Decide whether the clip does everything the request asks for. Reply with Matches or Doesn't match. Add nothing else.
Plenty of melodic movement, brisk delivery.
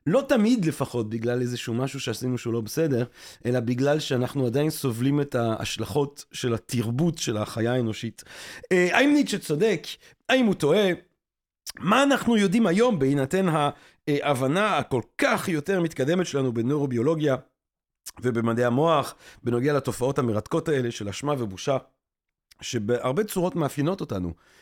Doesn't match